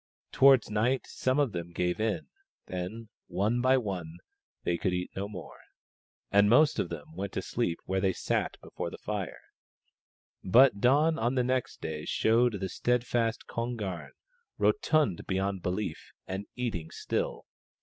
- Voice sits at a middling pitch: No, low, 105 Hz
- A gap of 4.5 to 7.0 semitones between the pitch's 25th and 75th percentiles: Yes, average, 5.1 semitones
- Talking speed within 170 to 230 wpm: No, average, 155 wpm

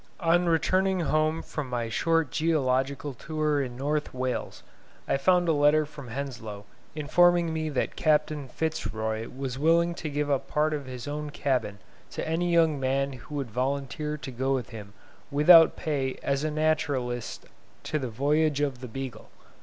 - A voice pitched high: No, medium, 145 Hz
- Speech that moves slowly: No, average, 165 wpm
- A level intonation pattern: No, average, 3.3 semitones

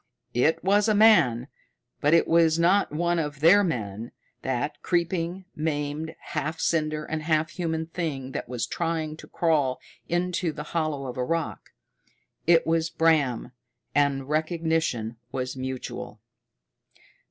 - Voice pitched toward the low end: No, medium, 155 Hz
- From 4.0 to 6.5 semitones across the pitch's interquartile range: No, average, 3.4 semitones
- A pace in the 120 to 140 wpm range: Yes, slow, 135 wpm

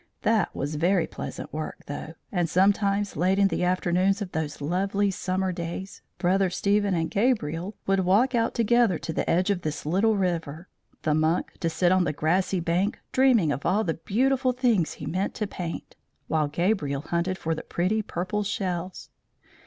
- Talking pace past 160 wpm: Yes, average, 175 wpm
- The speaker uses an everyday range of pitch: Yes, average, 3.4 semitones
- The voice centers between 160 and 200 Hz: Yes, medium, 185 Hz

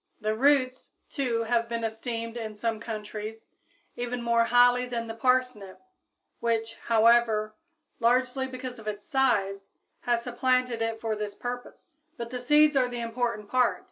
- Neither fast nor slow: Yes, average, 150 wpm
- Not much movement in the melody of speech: Yes, narrow, 2.0 semitones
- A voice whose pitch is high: Yes, high, 235 Hz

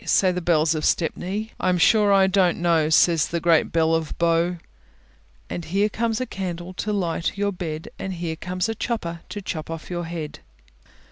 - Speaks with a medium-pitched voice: Yes, medium, 175 Hz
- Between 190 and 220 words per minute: Yes, average, 195 wpm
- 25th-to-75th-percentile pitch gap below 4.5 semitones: Yes, average, 2.9 semitones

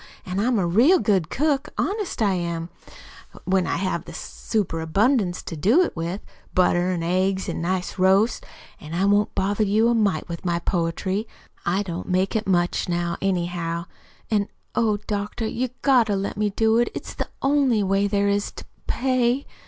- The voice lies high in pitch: Yes, high, 195 Hz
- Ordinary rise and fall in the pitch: Yes, average, 4.0 semitones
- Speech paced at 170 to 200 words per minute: Yes, average, 185 wpm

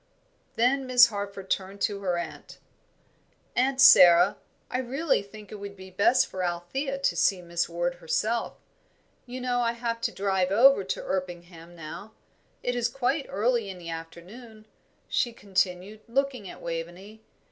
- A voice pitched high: Yes, high, 200 Hz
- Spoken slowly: No, average, 155 wpm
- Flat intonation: No, average, 5.3 semitones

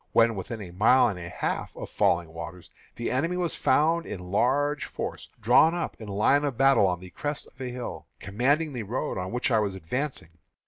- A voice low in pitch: Yes, low, 115 Hz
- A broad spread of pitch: Yes, wide, 7.2 semitones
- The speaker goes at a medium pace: No, fast, 210 wpm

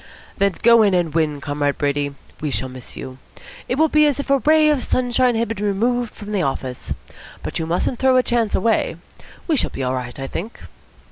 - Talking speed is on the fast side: Yes, fast, 215 wpm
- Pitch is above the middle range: Yes, high, 205 Hz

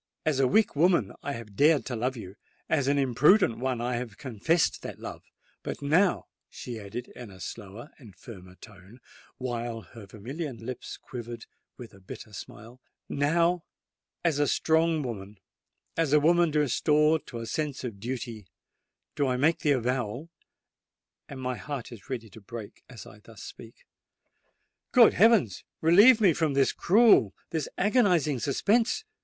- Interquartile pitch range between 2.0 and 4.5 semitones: No, wide, 5.6 semitones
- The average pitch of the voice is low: Yes, low, 130 Hz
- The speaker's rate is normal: Yes, average, 145 wpm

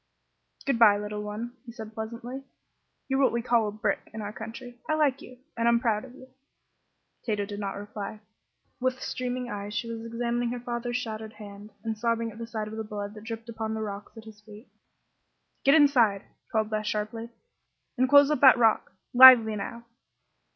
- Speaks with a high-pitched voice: Yes, high, 225 Hz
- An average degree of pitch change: No, narrow, 2.3 semitones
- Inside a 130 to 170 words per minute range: No, average, 190 wpm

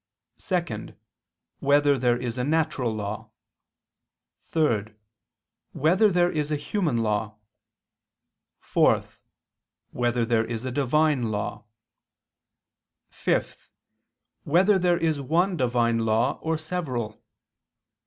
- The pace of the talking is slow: Yes, slow, 100 wpm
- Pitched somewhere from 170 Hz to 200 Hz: No, low, 135 Hz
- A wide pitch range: Yes, wide, 5.7 semitones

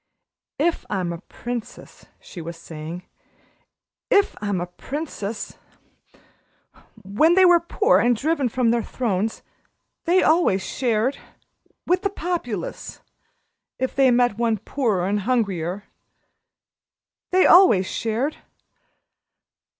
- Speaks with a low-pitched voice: No, high, 235 Hz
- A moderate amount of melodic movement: No, wide, 7.9 semitones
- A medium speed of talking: No, slow, 110 wpm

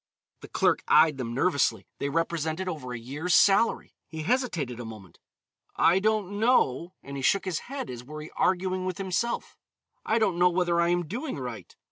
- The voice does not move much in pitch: No, wide, 5.4 semitones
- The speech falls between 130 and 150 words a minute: No, average, 185 wpm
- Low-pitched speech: No, medium, 170 Hz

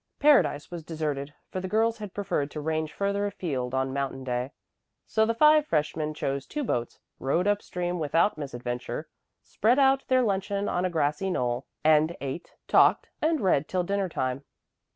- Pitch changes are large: Yes, wide, 6.5 semitones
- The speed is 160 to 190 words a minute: Yes, average, 175 wpm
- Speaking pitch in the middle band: Yes, medium, 165 Hz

